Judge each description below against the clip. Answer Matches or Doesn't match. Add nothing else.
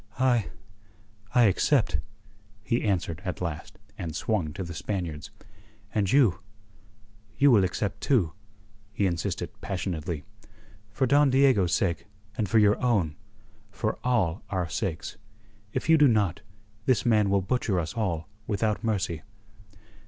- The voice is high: Doesn't match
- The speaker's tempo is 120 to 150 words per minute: Matches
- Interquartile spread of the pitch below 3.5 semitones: Doesn't match